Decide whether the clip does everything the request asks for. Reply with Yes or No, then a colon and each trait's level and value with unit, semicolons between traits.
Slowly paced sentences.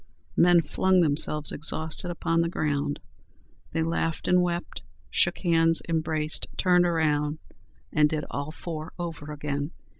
Yes: slow, 130 wpm